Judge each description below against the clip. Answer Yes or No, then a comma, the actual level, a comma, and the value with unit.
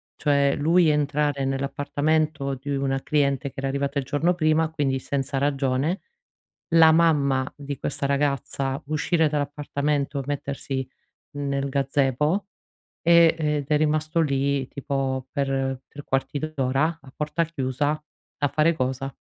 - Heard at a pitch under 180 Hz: Yes, medium, 140 Hz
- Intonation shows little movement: Yes, narrow, 2.0 semitones